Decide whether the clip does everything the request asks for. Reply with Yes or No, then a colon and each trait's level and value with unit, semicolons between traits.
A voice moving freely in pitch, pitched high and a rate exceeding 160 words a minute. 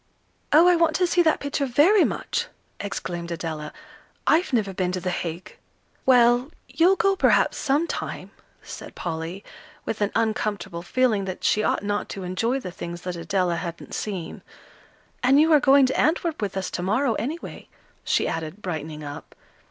Yes: wide, 8.2 semitones; high, 210 Hz; average, 170 wpm